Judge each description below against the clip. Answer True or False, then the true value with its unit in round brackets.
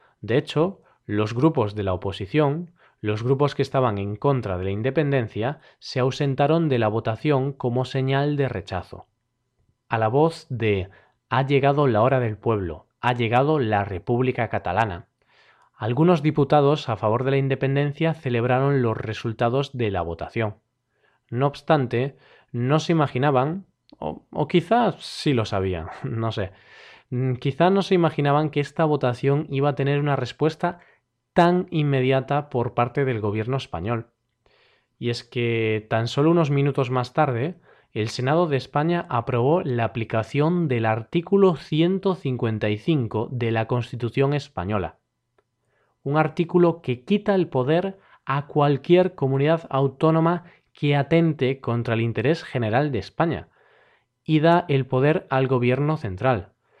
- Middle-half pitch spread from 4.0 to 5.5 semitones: True (4.6 semitones)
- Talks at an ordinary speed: True (140 wpm)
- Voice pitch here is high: False (135 Hz)